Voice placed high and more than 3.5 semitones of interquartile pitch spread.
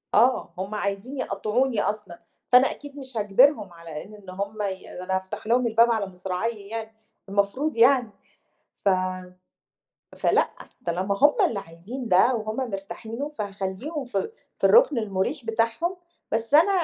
Yes: high, 220 Hz; average, 4.4 semitones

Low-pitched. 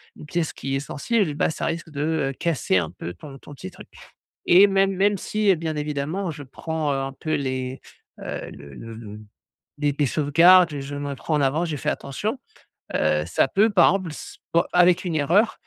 No: medium, 150 Hz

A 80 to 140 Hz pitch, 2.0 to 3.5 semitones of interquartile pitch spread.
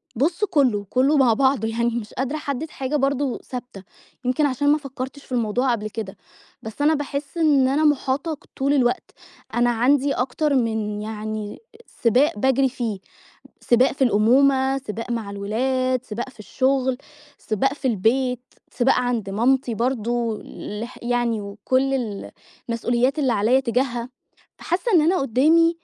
No: very high, 255 Hz; average, 3.2 semitones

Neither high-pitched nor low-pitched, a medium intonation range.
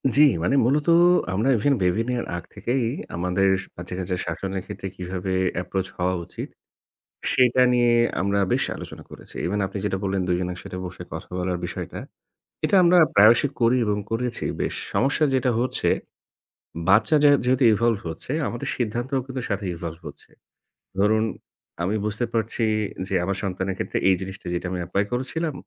No: low, 100 Hz; average, 4.9 semitones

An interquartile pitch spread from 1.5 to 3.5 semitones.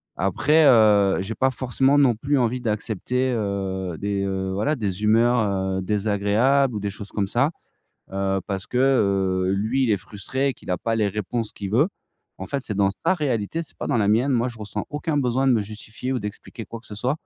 No: average, 4.5 semitones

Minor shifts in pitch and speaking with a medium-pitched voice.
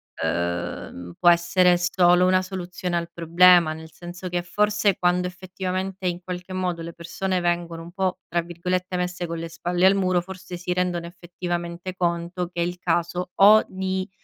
Yes: narrow, 1.3 semitones; medium, 180 Hz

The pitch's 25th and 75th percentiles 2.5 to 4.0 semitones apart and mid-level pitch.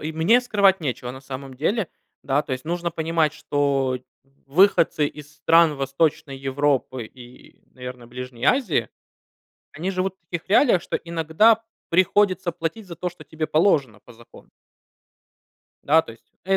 No: average, 4.8 semitones; medium, 155 Hz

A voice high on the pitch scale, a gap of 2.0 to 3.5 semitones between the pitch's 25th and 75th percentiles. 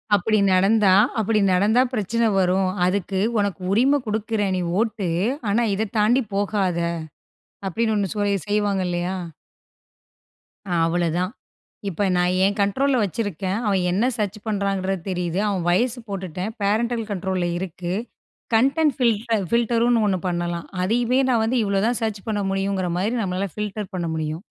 Yes: high, 200 Hz; average, 3.2 semitones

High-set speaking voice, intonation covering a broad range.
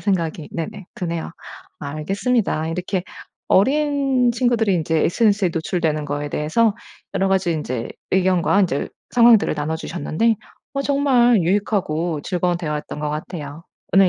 No: medium, 180 Hz; wide, 5.8 semitones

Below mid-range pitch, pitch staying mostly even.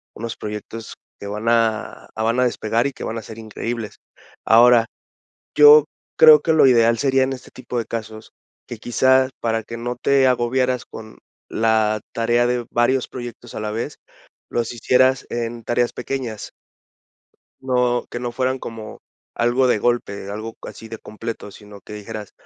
Yes: low, 120 Hz; narrow, 2.2 semitones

